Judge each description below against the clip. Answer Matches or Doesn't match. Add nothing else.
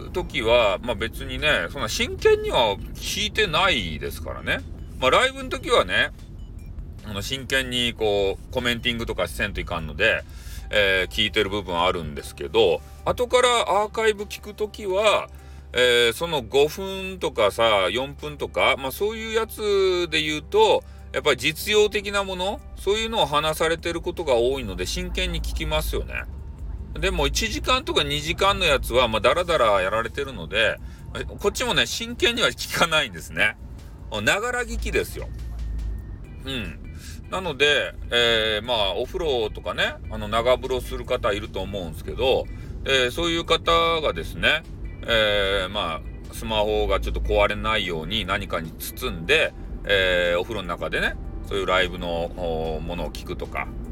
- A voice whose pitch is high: Doesn't match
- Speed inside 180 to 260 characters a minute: Doesn't match